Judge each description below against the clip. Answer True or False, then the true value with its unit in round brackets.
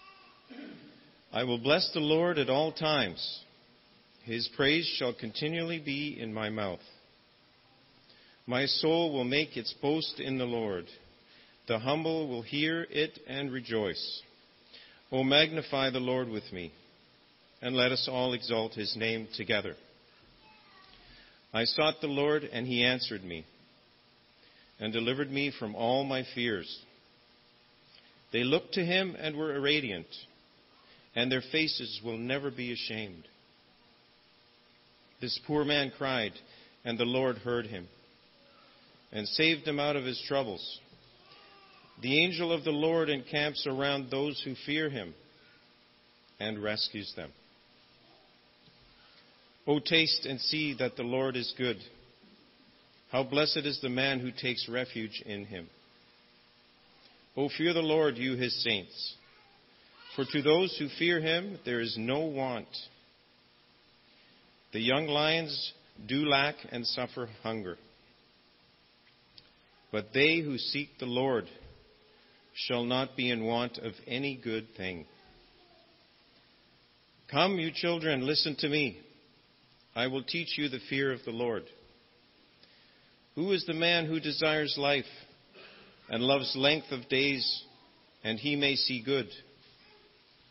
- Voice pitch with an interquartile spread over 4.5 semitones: True (5.6 semitones)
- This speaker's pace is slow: True (130 wpm)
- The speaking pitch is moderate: False (125 Hz)